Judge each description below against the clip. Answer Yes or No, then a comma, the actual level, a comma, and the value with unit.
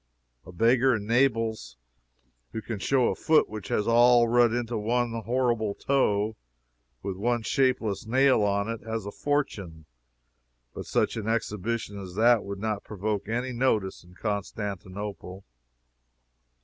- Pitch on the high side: No, low, 110 Hz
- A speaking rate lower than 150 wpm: Yes, average, 140 wpm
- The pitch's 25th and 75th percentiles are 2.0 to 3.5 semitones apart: Yes, average, 3.0 semitones